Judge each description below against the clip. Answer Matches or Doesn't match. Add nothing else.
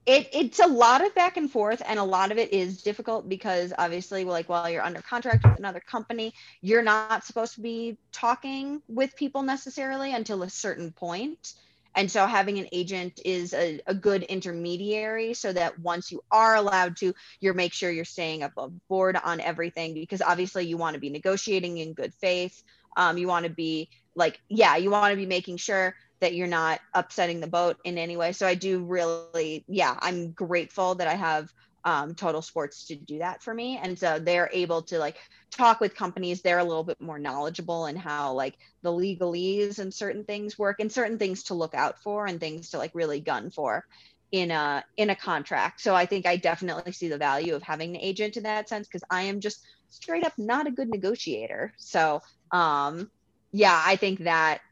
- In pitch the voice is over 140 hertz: Matches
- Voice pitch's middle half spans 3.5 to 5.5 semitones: Matches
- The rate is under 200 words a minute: Doesn't match